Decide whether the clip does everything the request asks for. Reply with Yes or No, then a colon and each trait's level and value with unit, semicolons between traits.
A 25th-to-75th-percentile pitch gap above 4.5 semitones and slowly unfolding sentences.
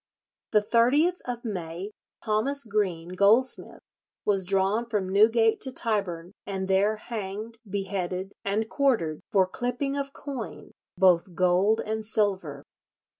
No: average, 3.5 semitones; slow, 125 wpm